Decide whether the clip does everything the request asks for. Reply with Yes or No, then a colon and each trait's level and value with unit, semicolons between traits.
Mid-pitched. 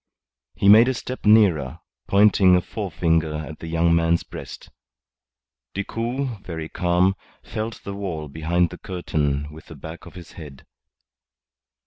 No: very low, 85 Hz